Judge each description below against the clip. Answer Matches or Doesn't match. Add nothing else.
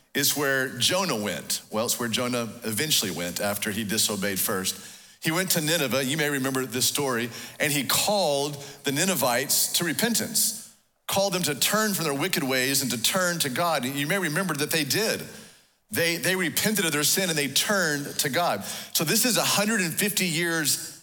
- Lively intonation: Matches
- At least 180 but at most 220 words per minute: Matches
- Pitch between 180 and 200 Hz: Doesn't match